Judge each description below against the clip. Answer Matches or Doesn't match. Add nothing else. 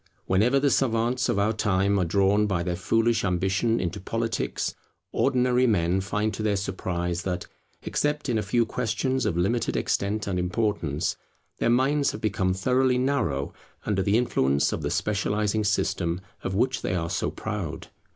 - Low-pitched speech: Matches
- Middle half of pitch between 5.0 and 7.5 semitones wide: Doesn't match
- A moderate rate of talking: Matches